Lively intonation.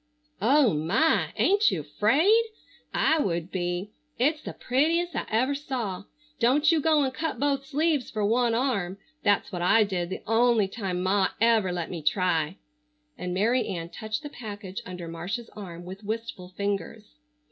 Yes: wide, 6.7 semitones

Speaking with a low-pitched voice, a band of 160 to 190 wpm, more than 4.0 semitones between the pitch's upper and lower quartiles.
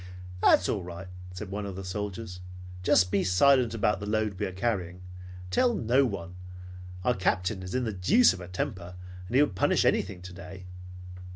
No: very low, 95 Hz; average, 180 wpm; average, 3.3 semitones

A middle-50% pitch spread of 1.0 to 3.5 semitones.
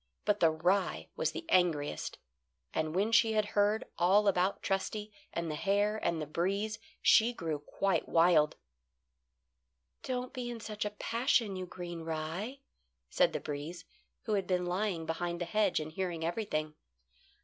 No: average, 4.3 semitones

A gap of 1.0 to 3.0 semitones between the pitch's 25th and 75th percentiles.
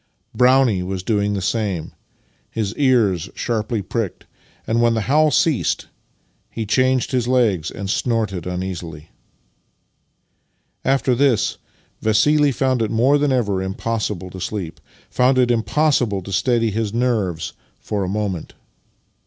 No: average, 4.7 semitones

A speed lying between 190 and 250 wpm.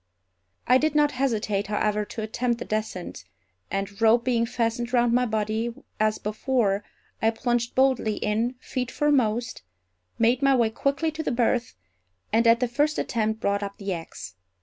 No: average, 170 wpm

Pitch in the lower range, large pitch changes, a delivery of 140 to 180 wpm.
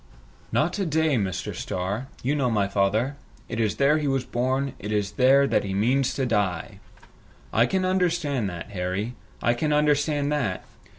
Yes: low, 125 Hz; wide, 6.0 semitones; average, 170 wpm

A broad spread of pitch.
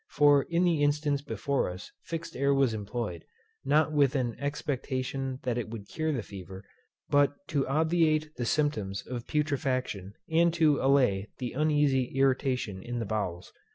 No: average, 4.1 semitones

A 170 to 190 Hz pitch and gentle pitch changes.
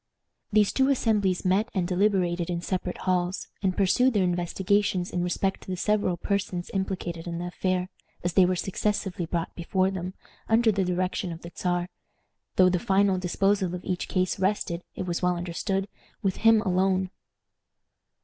Yes: medium, 185 Hz; narrow, 1.8 semitones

